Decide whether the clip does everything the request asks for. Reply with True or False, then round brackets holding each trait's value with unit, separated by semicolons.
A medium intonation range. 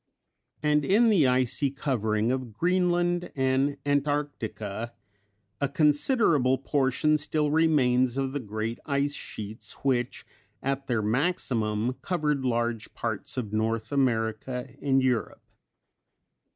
True (4.0 semitones)